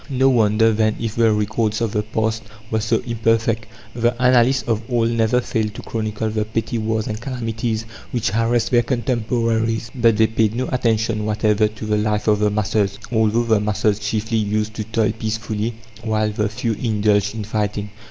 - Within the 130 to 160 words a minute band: No, average, 180 wpm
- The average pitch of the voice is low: Yes, low, 110 Hz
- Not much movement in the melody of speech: Yes, narrow, 1.3 semitones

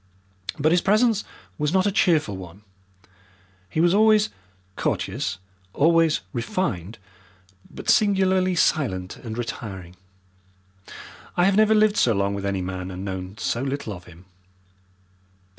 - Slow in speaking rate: Yes, slow, 130 wpm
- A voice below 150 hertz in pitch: Yes, medium, 140 Hz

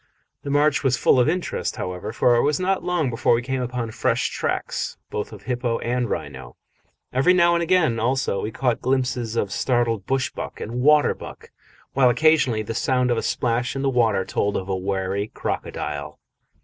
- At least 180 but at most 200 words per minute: Yes, average, 190 wpm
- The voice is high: No, low, 125 Hz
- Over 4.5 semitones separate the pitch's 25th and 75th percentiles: No, average, 3.6 semitones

